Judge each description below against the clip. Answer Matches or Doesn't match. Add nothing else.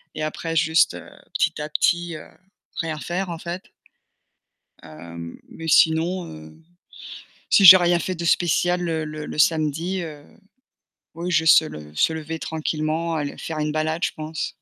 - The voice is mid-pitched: Matches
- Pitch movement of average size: Doesn't match